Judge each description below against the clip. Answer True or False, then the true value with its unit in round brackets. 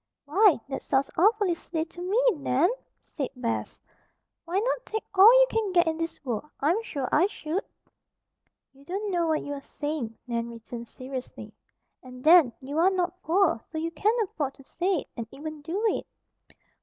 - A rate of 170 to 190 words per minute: True (180 wpm)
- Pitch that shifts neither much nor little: False (5.7 semitones)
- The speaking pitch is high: True (320 Hz)